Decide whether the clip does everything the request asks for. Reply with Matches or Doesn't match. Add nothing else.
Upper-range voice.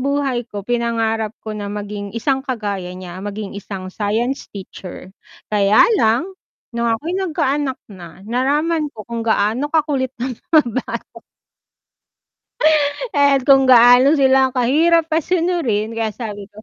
Matches